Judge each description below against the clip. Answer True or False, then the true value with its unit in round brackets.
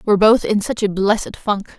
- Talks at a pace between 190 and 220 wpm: False (235 wpm)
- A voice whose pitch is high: True (205 Hz)